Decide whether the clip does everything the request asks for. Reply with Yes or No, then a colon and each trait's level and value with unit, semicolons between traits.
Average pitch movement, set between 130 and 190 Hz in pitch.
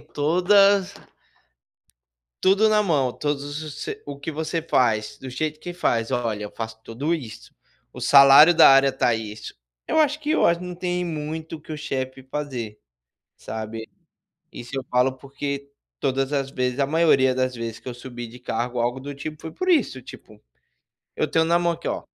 Yes: average, 4.6 semitones; medium, 140 Hz